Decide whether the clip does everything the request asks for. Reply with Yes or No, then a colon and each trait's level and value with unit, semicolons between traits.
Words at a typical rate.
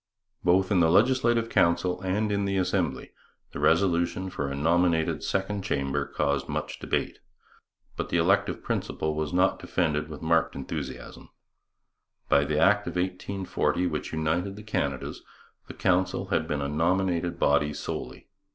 Yes: average, 150 wpm